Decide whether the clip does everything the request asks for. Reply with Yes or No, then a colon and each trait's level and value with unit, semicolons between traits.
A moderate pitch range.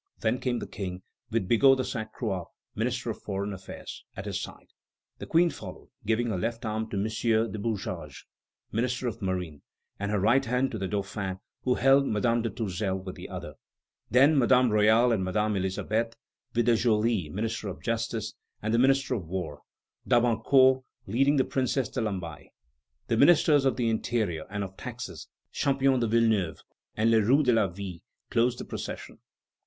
Yes: average, 3.8 semitones